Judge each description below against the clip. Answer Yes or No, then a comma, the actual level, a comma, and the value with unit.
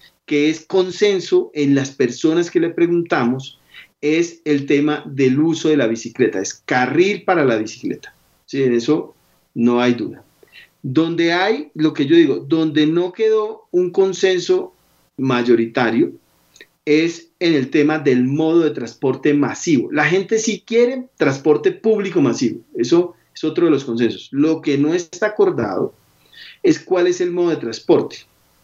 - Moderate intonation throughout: No, wide, 8.2 semitones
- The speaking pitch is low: No, medium, 160 Hz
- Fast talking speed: No, average, 155 wpm